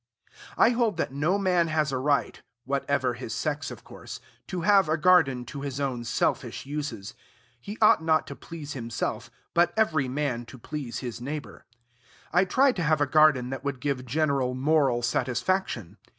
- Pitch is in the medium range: Yes, medium, 145 Hz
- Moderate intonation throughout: Yes, average, 4.3 semitones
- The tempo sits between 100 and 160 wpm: No, average, 175 wpm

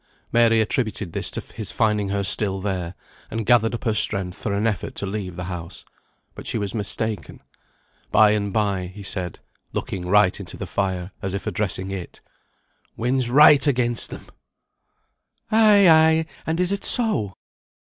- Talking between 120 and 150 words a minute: No, average, 165 wpm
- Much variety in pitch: No, average, 3.8 semitones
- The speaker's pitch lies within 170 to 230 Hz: No, low, 105 Hz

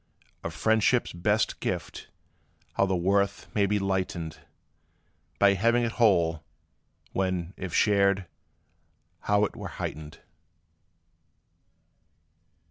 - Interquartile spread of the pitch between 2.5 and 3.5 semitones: Yes, average, 2.9 semitones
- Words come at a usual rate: No, slow, 100 wpm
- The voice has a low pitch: Yes, low, 100 Hz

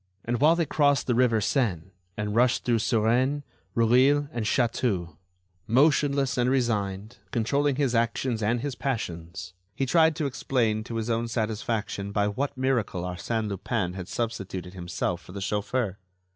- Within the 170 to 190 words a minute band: No, average, 155 wpm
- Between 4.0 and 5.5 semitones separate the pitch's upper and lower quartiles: Yes, average, 4.3 semitones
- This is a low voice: Yes, low, 115 Hz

